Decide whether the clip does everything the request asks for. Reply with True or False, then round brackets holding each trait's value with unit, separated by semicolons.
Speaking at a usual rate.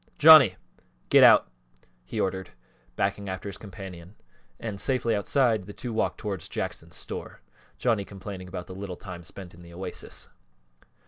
True (150 wpm)